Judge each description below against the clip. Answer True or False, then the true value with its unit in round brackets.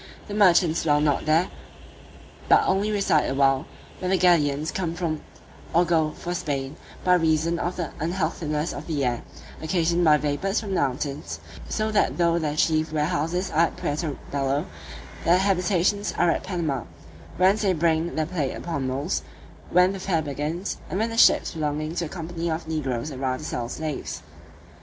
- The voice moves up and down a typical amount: True (3.2 semitones)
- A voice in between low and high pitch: True (160 Hz)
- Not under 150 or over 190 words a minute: True (175 wpm)